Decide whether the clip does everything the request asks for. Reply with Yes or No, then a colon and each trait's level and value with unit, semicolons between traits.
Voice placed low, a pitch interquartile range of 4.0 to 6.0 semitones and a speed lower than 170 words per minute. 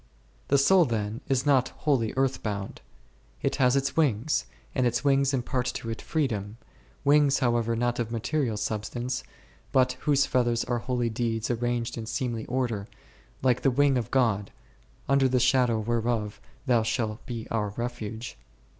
No: low, 120 Hz; average, 2.8 semitones; average, 155 wpm